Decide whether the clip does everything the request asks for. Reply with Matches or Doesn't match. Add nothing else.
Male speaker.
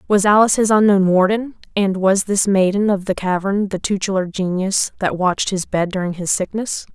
Doesn't match